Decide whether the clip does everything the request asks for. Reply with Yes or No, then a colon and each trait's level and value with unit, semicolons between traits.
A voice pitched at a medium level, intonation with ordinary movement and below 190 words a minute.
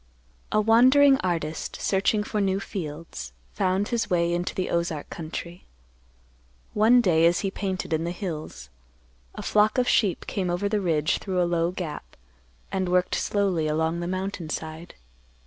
Yes: medium, 180 Hz; average, 3.4 semitones; average, 160 wpm